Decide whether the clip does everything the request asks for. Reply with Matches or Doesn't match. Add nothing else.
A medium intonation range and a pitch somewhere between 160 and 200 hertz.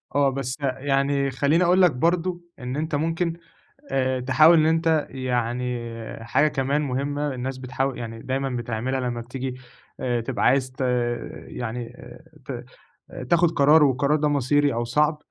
Doesn't match